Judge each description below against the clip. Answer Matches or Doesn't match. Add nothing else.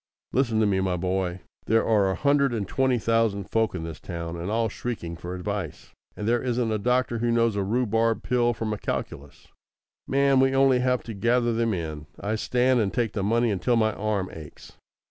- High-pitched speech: Doesn't match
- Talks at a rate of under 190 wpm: Doesn't match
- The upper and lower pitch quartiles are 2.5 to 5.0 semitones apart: Matches